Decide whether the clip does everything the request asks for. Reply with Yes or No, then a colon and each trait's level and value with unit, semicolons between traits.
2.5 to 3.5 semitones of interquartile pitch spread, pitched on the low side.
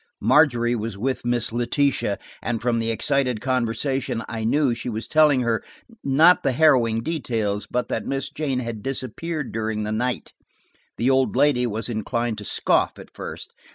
Yes: average, 3.2 semitones; low, 120 Hz